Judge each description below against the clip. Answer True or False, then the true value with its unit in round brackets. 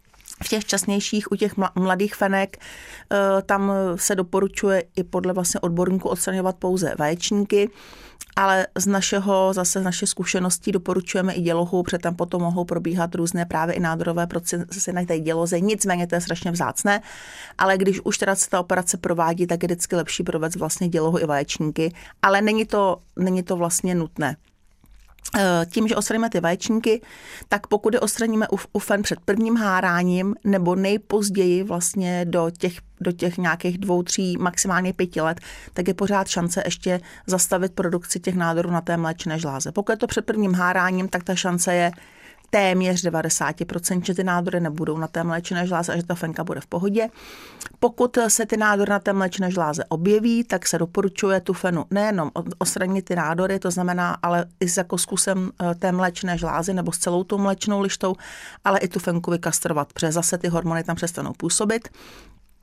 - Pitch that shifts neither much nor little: False (2.3 semitones)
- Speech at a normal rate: False (175 wpm)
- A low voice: False (185 Hz)